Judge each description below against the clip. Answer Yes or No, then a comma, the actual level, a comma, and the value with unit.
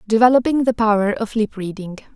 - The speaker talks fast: No, average, 165 wpm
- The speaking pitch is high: Yes, high, 220 Hz